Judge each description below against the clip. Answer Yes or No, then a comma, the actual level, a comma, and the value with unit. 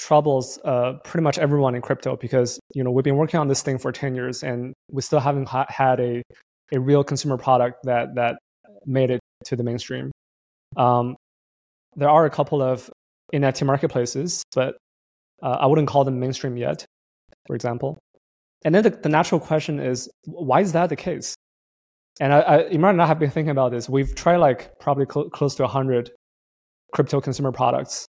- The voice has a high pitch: No, low, 135 Hz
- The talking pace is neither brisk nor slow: Yes, average, 190 wpm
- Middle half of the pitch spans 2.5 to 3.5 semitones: Yes, average, 3.0 semitones